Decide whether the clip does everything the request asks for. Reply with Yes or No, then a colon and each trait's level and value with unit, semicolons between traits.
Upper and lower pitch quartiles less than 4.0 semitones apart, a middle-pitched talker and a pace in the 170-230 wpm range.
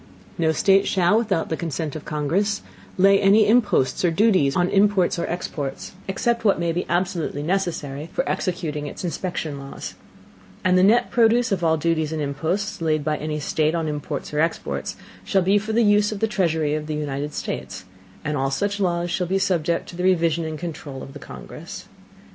No: average, 4.3 semitones; medium, 170 Hz; average, 195 wpm